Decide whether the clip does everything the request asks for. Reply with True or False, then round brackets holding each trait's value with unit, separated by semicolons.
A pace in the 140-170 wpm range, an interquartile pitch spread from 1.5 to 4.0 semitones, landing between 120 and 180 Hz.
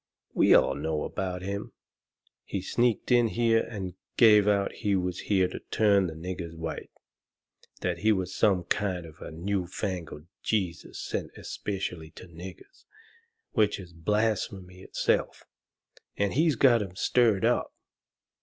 False (145 wpm; 3.0 semitones; 95 Hz)